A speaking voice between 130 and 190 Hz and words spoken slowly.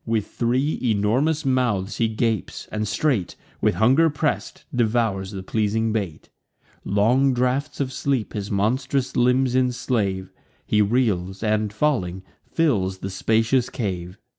No: low, 115 Hz; slow, 130 wpm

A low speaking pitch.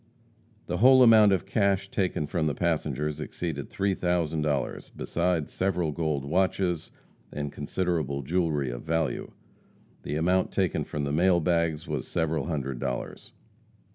Yes: very low, 85 Hz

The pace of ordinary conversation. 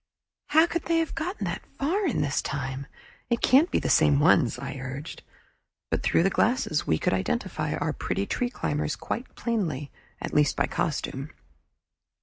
Yes: average, 170 wpm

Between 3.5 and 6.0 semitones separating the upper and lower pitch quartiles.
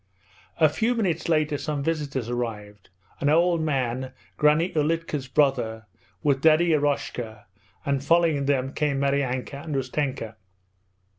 No: average, 3.1 semitones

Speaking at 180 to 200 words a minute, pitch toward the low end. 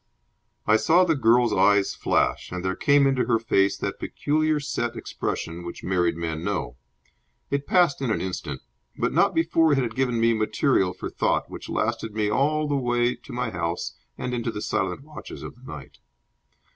Yes: average, 185 wpm; low, 115 Hz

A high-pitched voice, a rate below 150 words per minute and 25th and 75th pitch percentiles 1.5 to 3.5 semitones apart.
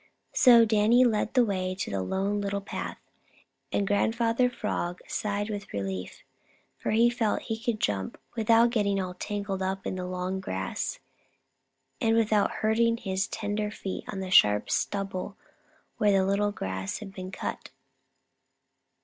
Yes: high, 200 Hz; average, 140 wpm; average, 2.9 semitones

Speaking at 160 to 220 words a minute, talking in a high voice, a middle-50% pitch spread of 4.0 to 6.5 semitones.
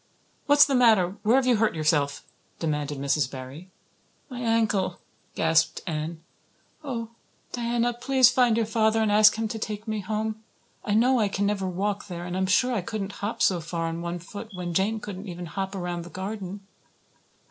Yes: average, 185 wpm; high, 205 Hz; average, 4.4 semitones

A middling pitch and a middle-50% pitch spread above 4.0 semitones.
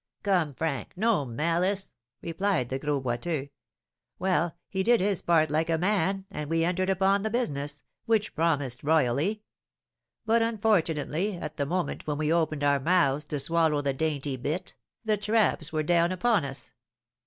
Yes: medium, 165 Hz; average, 4.9 semitones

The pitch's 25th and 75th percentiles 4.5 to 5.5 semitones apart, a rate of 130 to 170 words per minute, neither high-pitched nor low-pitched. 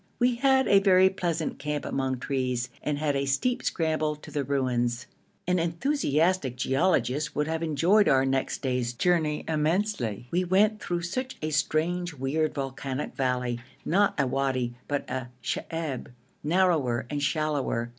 Yes: average, 4.9 semitones; average, 150 wpm; medium, 150 Hz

